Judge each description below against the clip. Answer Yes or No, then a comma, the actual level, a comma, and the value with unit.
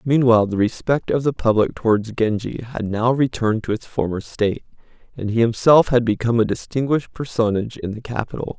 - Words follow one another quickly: No, average, 180 wpm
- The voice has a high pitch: No, low, 115 Hz